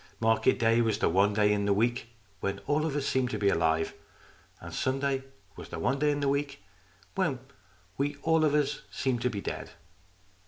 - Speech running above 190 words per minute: Yes, fast, 205 wpm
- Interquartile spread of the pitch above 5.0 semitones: Yes, wide, 5.4 semitones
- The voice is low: Yes, low, 125 Hz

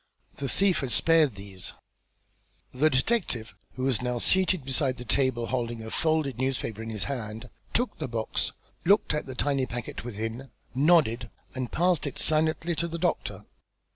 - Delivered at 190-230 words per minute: No, average, 165 wpm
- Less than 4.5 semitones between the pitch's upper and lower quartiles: No, average, 5.1 semitones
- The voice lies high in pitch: No, low, 130 Hz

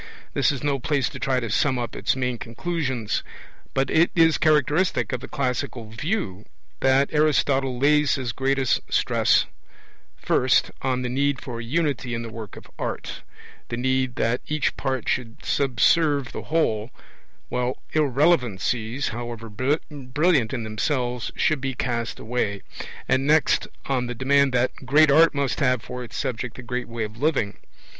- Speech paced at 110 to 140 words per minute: No, average, 160 wpm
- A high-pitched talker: No, low, 130 Hz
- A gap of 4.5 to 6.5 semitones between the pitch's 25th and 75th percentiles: No, average, 3.1 semitones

